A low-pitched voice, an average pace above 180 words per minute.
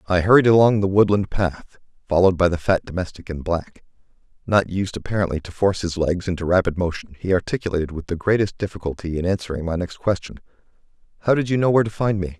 Yes: very low, 95 Hz; fast, 205 wpm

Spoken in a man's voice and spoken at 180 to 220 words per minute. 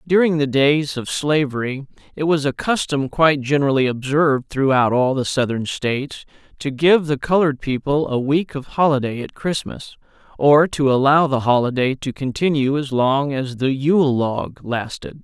No: male; average, 165 wpm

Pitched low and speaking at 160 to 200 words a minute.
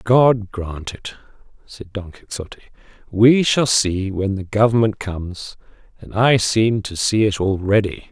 No: low, 105 Hz; average, 150 wpm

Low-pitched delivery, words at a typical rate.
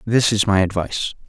Yes: low, 100 Hz; average, 190 wpm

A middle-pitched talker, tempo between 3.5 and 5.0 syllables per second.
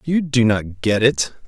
No: low, 120 Hz; 4.0 syllables/s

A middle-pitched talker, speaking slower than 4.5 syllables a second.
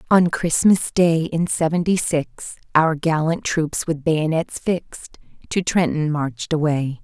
Yes: medium, 160 Hz; 4.0 syllables/s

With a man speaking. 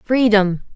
No: female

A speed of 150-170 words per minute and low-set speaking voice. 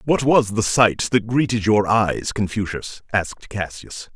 Yes: average, 160 wpm; low, 110 Hz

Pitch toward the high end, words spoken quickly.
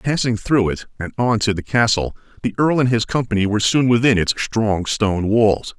No: low, 110 Hz; fast, 210 wpm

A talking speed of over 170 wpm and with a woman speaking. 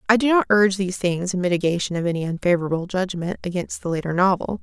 Yes: fast, 205 wpm; female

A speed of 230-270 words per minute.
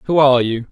Yes: fast, 250 wpm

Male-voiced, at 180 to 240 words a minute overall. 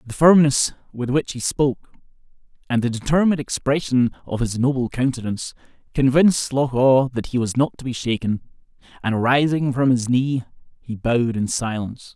No: male; average, 165 wpm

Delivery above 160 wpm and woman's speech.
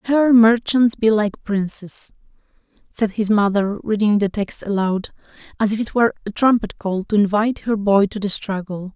Yes: average, 175 wpm; female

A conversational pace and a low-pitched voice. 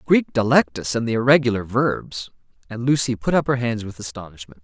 Yes: average, 180 wpm; low, 120 Hz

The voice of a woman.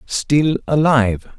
No: male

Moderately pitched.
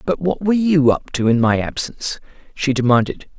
Yes: medium, 145 Hz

